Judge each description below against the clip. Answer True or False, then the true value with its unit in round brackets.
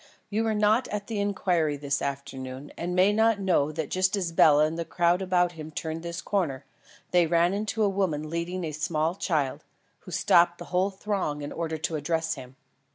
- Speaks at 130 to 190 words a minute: False (200 wpm)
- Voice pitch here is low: False (170 Hz)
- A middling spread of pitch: True (3.9 semitones)